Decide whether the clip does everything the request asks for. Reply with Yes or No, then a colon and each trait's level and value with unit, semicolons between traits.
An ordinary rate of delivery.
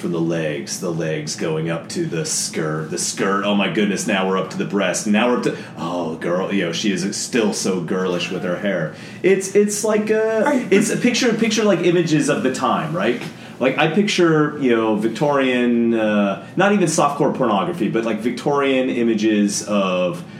Yes: average, 195 wpm